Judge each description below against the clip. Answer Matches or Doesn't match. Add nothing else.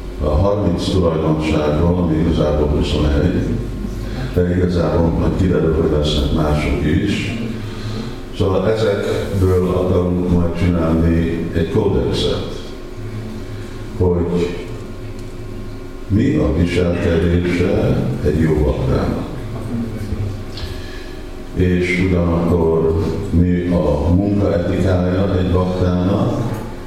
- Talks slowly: Matches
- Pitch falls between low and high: Doesn't match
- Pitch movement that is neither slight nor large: Matches